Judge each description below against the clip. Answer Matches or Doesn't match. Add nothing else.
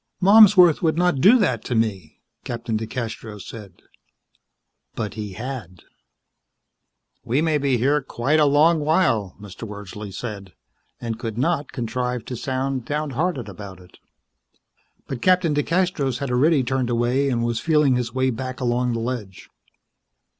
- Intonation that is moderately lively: Matches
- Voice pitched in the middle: Doesn't match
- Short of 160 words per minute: Matches